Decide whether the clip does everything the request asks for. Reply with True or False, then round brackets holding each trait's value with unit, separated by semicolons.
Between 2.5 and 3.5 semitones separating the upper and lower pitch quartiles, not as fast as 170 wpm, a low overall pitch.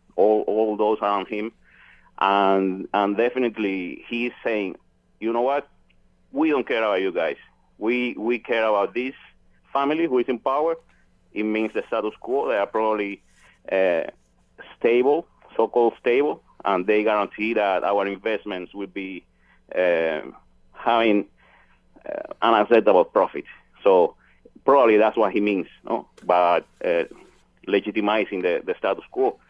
False (5.6 semitones; 140 wpm; 110 Hz)